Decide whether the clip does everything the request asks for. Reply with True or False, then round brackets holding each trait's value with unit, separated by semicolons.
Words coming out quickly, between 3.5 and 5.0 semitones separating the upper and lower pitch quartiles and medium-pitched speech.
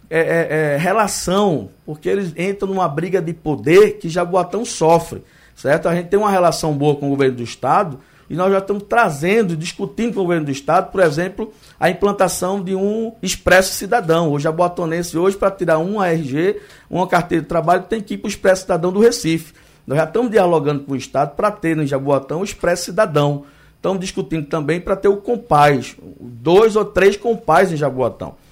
True (195 wpm; 4.0 semitones; 175 Hz)